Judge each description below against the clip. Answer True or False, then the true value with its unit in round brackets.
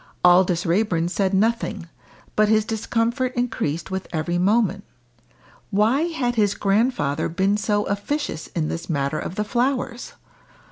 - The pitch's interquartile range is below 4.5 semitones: False (4.8 semitones)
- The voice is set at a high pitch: True (205 Hz)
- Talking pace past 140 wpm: False (135 wpm)